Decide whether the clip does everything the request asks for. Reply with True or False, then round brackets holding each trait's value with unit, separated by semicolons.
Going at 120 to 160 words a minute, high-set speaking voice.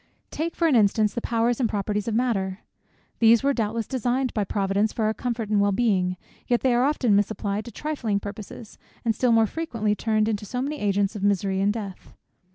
False (205 wpm; 220 Hz)